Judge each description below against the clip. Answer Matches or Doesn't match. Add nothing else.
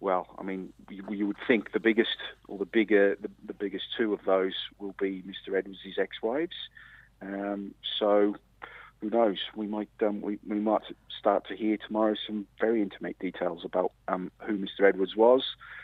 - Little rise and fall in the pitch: Matches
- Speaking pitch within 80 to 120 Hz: Matches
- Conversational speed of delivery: Matches